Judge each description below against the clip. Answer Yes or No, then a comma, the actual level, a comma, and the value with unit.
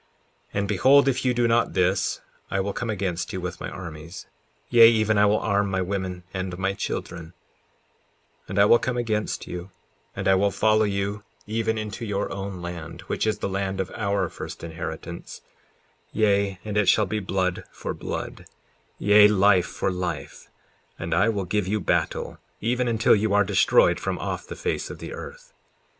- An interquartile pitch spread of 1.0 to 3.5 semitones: Yes, average, 2.7 semitones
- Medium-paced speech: Yes, average, 185 wpm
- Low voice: Yes, low, 100 Hz